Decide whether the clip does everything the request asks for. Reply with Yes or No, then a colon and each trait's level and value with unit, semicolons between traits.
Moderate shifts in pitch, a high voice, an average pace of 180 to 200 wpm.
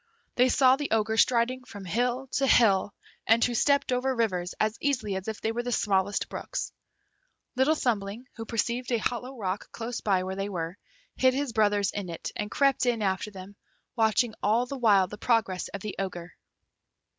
Yes: average, 3.9 semitones; high, 225 Hz; average, 190 wpm